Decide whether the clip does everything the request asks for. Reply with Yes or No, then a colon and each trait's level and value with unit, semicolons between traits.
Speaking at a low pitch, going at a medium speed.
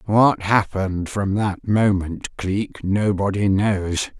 No: low, 100 Hz; slow, 115 wpm